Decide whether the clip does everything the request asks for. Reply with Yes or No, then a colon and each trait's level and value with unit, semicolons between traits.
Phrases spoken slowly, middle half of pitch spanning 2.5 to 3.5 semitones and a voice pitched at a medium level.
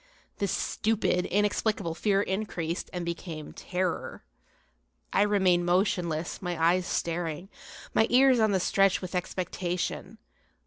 Yes: slow, 120 wpm; average, 2.8 semitones; medium, 180 Hz